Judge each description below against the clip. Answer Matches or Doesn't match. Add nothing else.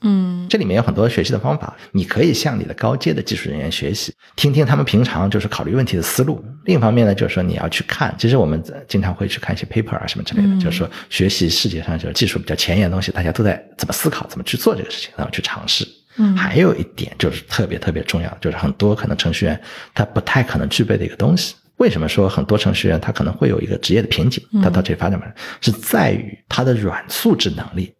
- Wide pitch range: Matches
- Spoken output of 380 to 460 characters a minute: Matches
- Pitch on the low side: Matches